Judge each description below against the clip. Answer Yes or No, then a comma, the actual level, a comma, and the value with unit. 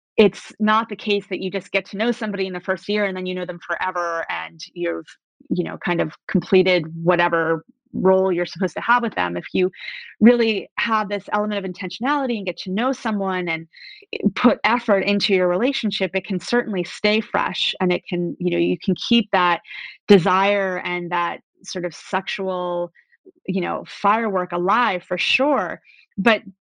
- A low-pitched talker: No, high, 190 Hz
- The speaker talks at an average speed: Yes, average, 185 wpm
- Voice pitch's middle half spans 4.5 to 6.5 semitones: No, average, 3.2 semitones